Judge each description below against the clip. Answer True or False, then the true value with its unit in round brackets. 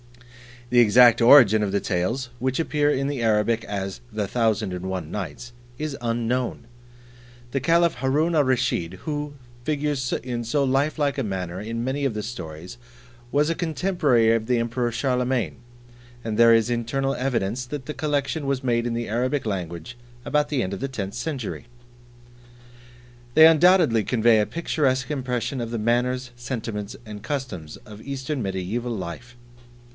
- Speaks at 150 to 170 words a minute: True (160 wpm)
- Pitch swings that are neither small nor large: True (4.0 semitones)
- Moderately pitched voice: False (120 Hz)